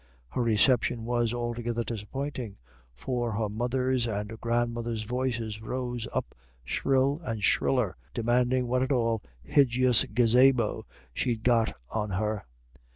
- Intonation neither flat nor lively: No, narrow, 2.2 semitones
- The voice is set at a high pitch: No, low, 120 Hz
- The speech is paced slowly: Yes, slow, 120 wpm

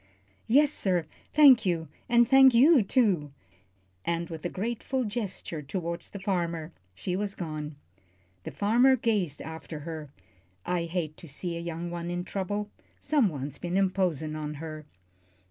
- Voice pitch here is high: No, medium, 175 Hz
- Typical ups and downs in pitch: Yes, average, 4.5 semitones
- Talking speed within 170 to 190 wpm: No, average, 145 wpm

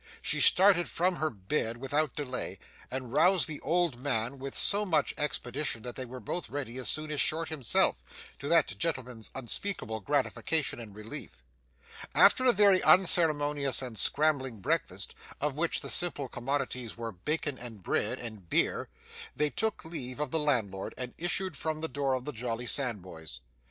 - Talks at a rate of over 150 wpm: Yes, average, 165 wpm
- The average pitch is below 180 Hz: Yes, medium, 140 Hz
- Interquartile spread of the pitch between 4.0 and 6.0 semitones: Yes, average, 4.9 semitones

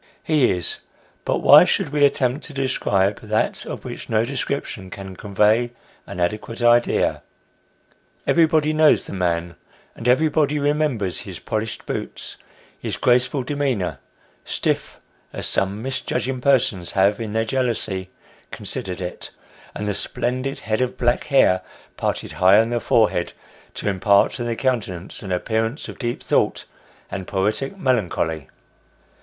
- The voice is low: Yes, low, 115 Hz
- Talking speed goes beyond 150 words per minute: No, average, 140 wpm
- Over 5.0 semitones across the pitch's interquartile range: Yes, wide, 5.4 semitones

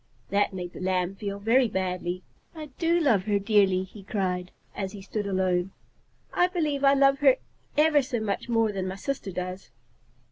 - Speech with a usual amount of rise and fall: No, wide, 6.2 semitones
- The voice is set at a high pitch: Yes, high, 200 Hz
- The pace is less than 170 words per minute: No, average, 180 wpm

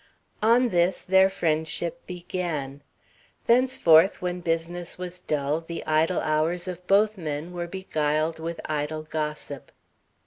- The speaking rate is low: Yes, slow, 125 wpm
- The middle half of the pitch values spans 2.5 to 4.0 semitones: Yes, average, 2.8 semitones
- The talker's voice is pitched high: No, medium, 170 Hz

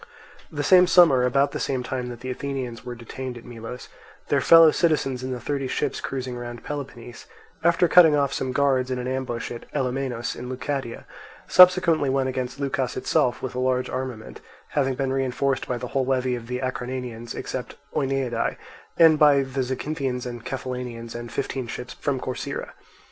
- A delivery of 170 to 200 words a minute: Yes, average, 175 wpm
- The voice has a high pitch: No, low, 130 Hz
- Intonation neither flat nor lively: No, narrow, 1.9 semitones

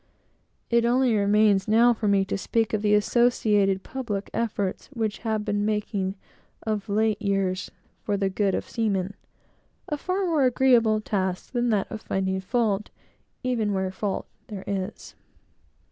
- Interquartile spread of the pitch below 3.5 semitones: Yes, average, 2.9 semitones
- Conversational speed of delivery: Yes, average, 150 wpm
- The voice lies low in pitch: No, high, 210 Hz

